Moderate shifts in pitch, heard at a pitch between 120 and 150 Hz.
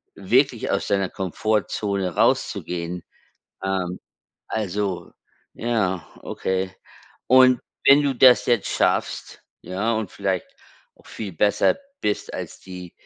No: average, 3.4 semitones; low, 100 Hz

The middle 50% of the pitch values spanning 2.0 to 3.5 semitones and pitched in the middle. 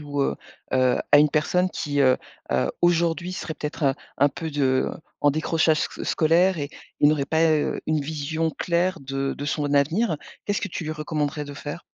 Yes: narrow, 2.4 semitones; medium, 150 Hz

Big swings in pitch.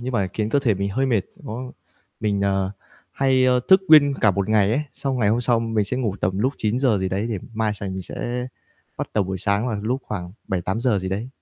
No: average, 4.2 semitones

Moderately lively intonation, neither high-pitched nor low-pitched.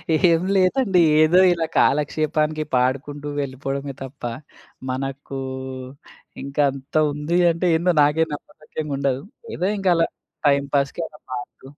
Yes: average, 3.2 semitones; medium, 150 Hz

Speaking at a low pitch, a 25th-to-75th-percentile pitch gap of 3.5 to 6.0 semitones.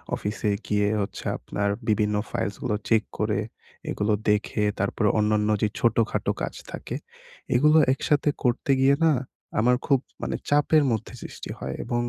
Yes: low, 110 Hz; average, 3.8 semitones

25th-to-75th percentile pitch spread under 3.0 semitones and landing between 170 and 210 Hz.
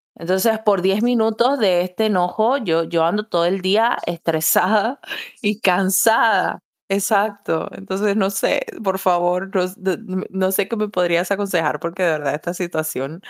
No: average, 3.3 semitones; high, 190 Hz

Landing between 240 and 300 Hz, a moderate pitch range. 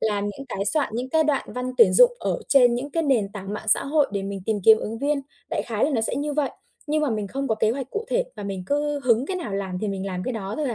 No: high, 245 Hz; wide, 5.9 semitones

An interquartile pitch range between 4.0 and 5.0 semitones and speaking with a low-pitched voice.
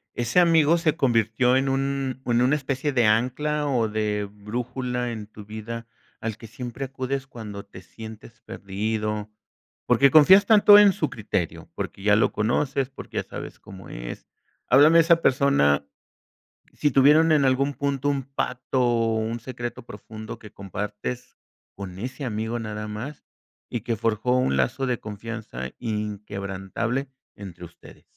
Yes: average, 4.3 semitones; low, 120 Hz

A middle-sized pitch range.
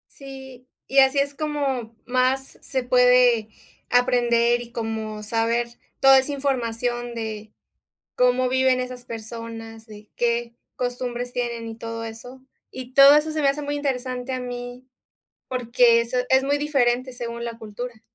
No: narrow, 2.0 semitones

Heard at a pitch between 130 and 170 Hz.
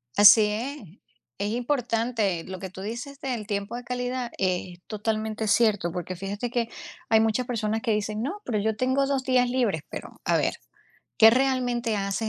No: high, 225 Hz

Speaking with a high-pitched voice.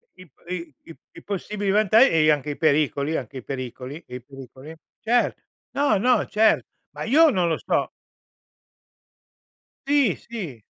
No: medium, 165 Hz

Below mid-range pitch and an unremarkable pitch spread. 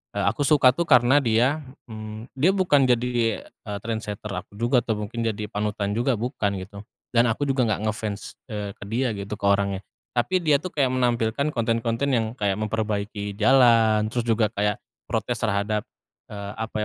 Yes: low, 115 Hz; average, 3.1 semitones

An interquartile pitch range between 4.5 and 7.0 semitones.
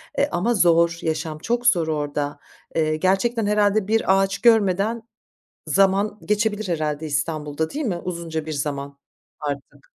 Yes: average, 5.1 semitones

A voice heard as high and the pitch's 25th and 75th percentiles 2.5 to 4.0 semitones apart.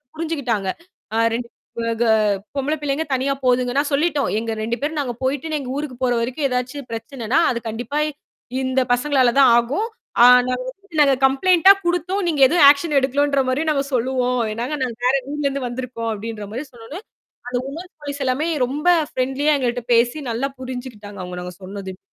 Yes: very high, 260 Hz; average, 3.4 semitones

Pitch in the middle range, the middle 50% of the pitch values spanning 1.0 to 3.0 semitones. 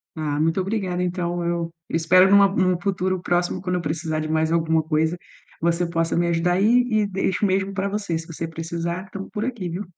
Yes: medium, 175 Hz; narrow, 2.5 semitones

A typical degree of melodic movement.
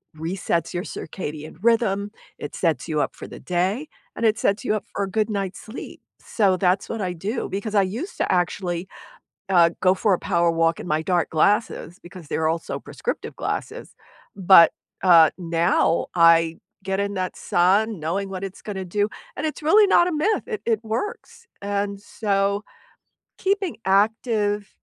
Yes: average, 3.7 semitones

